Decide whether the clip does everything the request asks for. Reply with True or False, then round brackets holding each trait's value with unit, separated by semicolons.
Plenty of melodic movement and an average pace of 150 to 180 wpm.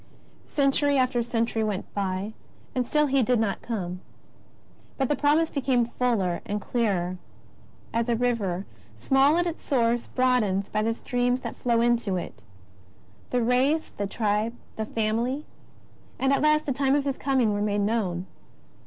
False (4.3 semitones; 160 wpm)